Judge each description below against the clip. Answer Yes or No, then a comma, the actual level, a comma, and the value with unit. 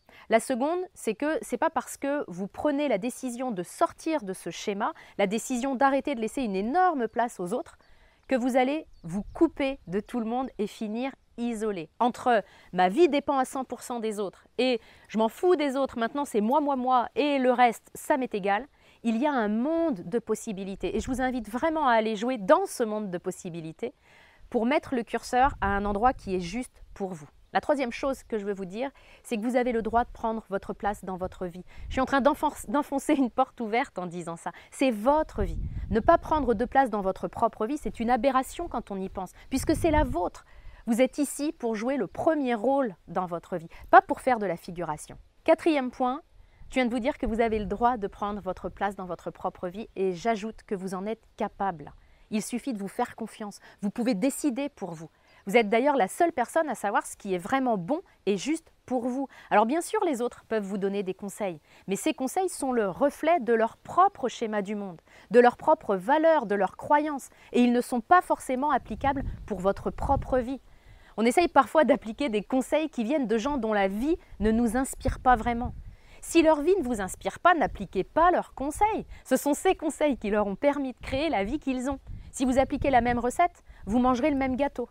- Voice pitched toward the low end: No, high, 245 Hz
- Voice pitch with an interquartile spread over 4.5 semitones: Yes, average, 5.2 semitones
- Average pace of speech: No, fast, 225 wpm